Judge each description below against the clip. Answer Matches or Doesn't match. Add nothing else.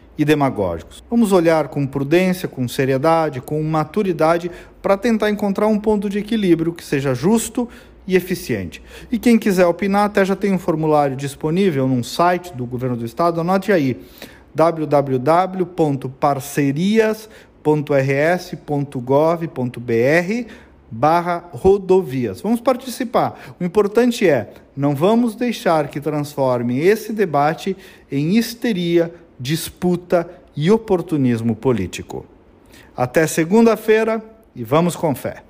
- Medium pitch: Matches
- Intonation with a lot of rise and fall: Matches